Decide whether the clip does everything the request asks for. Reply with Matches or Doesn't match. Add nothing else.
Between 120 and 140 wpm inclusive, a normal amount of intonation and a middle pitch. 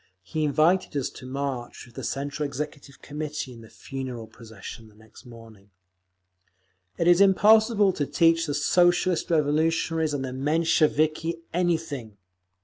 Matches